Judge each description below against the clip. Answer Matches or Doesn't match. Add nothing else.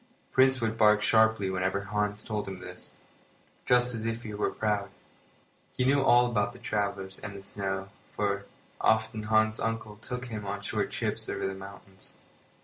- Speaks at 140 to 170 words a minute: Matches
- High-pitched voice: Doesn't match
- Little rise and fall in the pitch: Matches